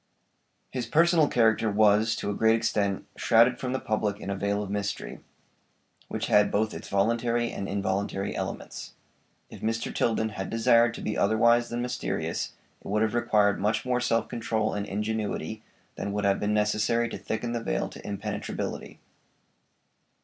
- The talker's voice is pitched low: Yes, low, 110 Hz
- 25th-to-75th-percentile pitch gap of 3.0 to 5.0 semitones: No, narrow, 2.4 semitones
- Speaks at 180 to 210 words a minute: No, average, 165 wpm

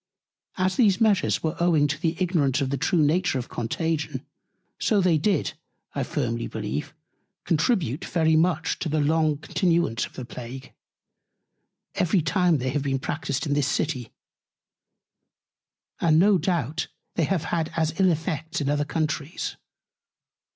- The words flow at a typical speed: Yes, average, 150 wpm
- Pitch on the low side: No, medium, 160 Hz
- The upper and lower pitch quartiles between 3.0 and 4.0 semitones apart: Yes, average, 3.5 semitones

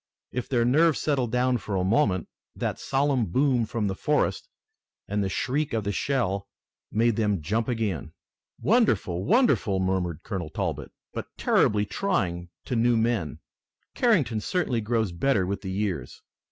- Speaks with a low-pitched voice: Yes, low, 110 Hz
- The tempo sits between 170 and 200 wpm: No, average, 155 wpm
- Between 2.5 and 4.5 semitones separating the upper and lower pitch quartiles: No, average, 5.1 semitones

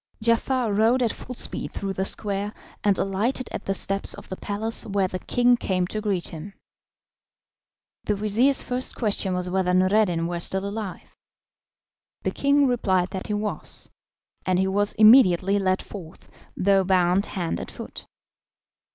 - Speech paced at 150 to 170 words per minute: Yes, average, 160 wpm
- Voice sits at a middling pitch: No, high, 200 Hz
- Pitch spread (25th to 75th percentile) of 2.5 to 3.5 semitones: Yes, average, 2.8 semitones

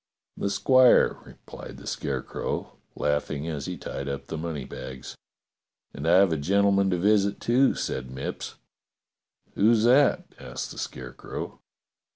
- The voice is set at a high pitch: No, very low, 85 Hz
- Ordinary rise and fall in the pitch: No, wide, 6.4 semitones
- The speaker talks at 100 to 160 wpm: Yes, average, 140 wpm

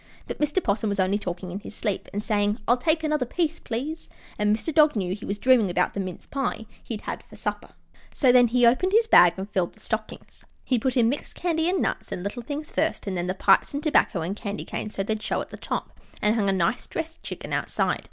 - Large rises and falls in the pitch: Yes, wide, 6.8 semitones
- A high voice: Yes, high, 225 Hz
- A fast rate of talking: Yes, fast, 245 wpm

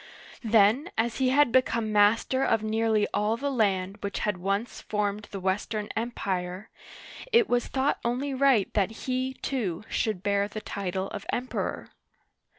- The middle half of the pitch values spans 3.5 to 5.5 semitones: Yes, average, 4.0 semitones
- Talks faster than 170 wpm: No, average, 155 wpm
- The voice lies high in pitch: Yes, high, 215 Hz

